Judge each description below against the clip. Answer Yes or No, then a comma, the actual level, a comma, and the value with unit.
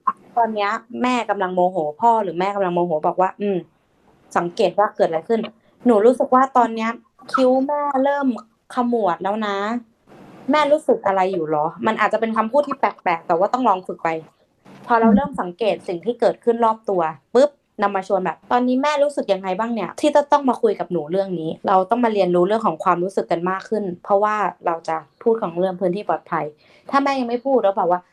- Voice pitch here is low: No, high, 210 Hz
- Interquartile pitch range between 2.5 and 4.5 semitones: No, average, 5.0 semitones